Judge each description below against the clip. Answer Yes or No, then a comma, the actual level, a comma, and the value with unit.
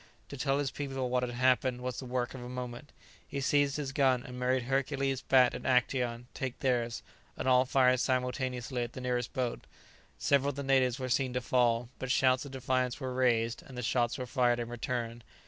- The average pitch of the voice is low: Yes, low, 125 Hz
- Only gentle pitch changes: Yes, narrow, 1.3 semitones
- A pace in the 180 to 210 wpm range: Yes, fast, 205 wpm